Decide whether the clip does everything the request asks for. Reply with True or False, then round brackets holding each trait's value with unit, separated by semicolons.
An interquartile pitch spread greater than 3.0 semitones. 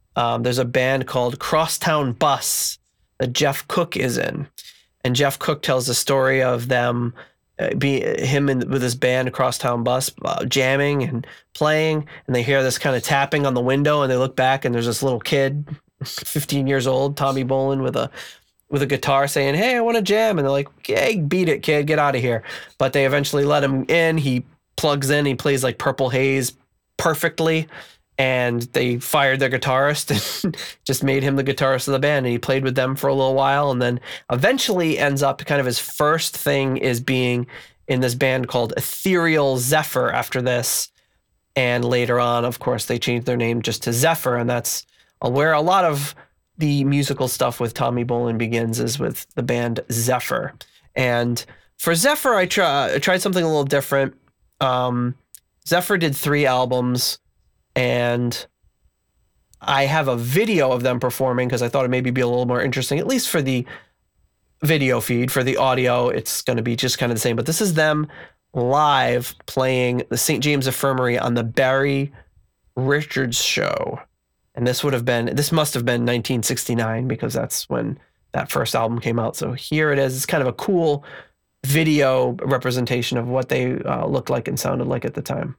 False (2.7 semitones)